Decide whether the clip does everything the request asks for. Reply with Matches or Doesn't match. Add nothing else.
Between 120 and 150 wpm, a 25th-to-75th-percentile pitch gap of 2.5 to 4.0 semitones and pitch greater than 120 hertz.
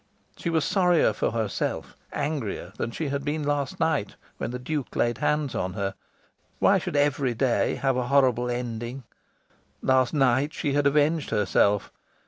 Doesn't match